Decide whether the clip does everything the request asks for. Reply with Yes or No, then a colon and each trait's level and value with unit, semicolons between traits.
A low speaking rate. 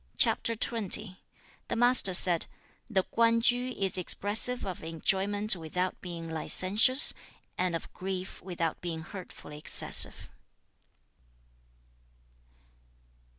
Yes: slow, 90 wpm